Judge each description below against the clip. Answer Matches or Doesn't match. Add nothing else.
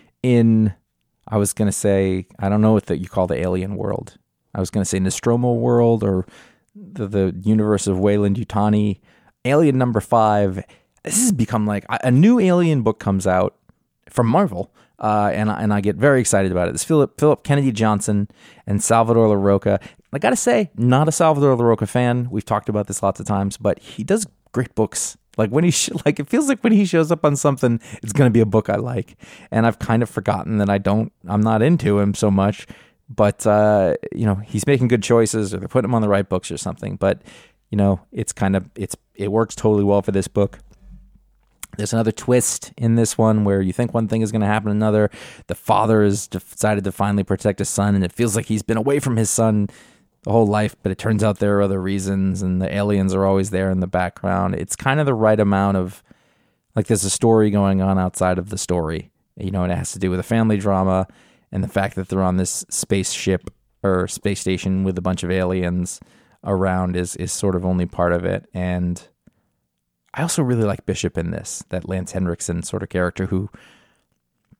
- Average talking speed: Doesn't match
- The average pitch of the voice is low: Matches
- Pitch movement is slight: Doesn't match